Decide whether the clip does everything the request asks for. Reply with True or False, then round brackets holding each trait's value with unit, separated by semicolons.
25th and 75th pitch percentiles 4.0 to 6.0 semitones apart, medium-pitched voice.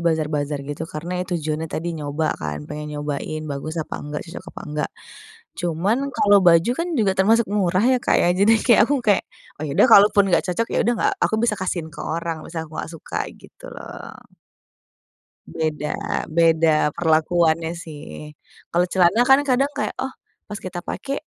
True (4.6 semitones; 170 Hz)